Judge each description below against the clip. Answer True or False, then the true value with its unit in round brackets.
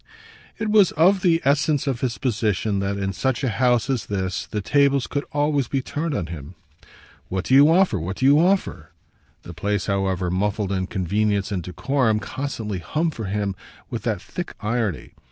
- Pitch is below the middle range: True (110 Hz)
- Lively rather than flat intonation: True (6.5 semitones)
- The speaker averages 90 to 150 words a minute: False (185 wpm)